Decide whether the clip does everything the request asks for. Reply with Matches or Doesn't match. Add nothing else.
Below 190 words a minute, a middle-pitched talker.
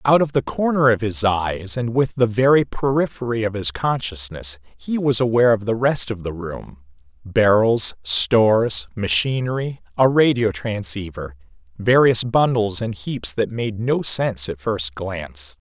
Doesn't match